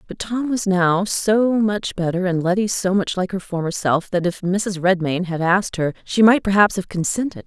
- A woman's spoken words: Yes, female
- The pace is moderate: No, fast, 215 wpm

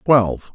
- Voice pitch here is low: Yes, low, 115 Hz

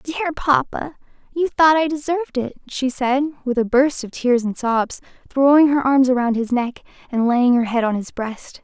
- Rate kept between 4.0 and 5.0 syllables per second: Yes, 4.7 syllables/s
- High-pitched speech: Yes, very high, 265 Hz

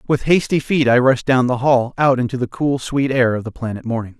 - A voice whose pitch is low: Yes, low, 130 Hz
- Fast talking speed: Yes, fast, 260 wpm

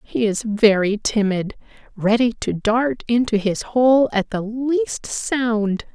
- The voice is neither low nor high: No, high, 225 Hz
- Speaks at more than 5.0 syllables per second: No, 3.3 syllables/s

